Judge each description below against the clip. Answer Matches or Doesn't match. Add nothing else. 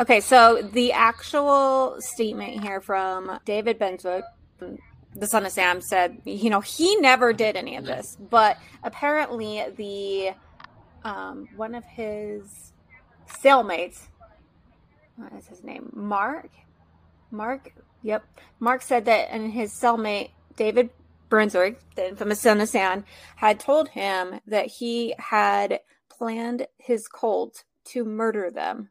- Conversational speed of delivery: Doesn't match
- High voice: Matches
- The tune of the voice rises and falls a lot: Doesn't match